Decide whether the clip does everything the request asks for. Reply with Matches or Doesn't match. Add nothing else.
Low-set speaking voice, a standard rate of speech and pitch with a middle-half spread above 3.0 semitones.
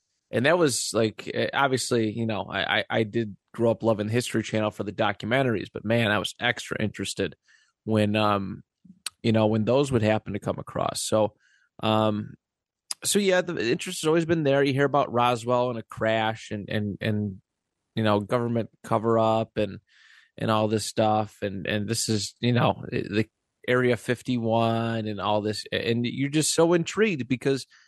Doesn't match